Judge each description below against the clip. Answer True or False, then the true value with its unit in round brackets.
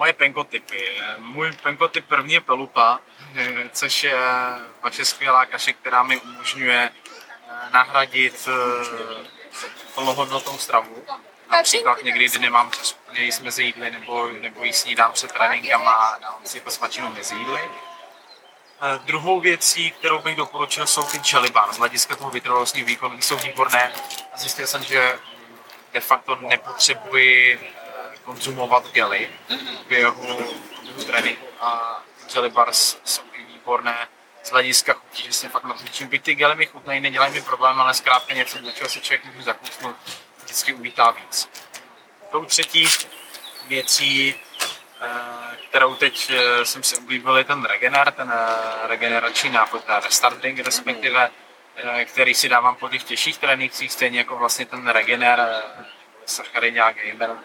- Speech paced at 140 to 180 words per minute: False (130 wpm)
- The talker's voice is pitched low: True (125 Hz)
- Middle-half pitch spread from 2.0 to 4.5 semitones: True (2.5 semitones)